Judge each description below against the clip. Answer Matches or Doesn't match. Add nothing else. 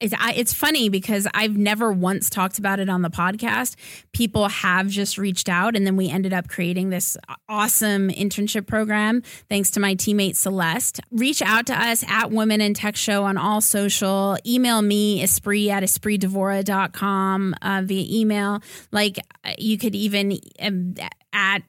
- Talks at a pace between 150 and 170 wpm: Matches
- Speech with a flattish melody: Matches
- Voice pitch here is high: Matches